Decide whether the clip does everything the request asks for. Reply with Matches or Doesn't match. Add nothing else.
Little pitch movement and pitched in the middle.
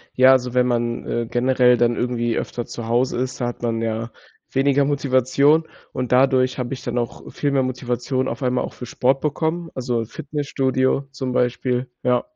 Doesn't match